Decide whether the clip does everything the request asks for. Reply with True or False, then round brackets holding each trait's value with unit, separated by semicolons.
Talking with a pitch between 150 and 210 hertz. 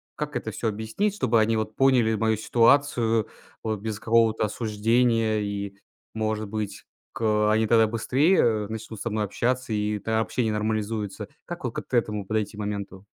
False (110 Hz)